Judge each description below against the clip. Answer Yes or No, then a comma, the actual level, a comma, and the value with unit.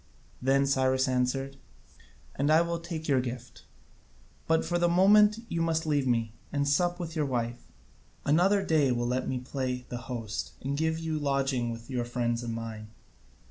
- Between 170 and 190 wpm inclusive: Yes, average, 180 wpm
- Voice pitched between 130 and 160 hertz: Yes, low, 135 Hz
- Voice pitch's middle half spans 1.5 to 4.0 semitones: No, average, 4.6 semitones